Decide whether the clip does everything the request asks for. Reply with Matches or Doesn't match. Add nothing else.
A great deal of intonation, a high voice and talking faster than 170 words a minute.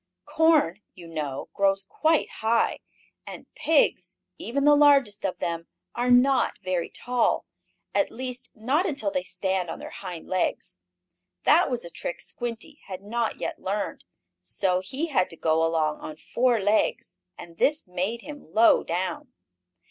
Doesn't match